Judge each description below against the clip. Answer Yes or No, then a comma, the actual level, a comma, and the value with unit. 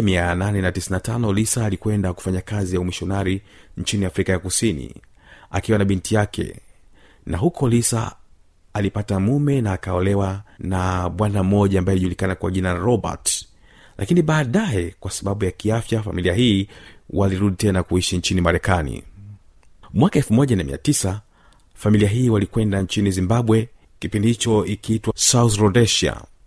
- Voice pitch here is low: Yes, low, 100 Hz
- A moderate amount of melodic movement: Yes, average, 3.2 semitones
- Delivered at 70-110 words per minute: No, average, 125 wpm